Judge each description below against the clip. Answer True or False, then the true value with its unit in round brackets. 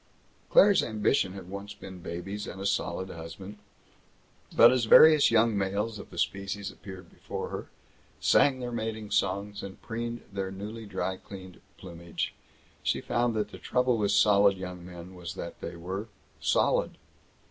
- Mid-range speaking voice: False (100 Hz)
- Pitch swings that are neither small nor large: True (3.0 semitones)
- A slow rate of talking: False (160 wpm)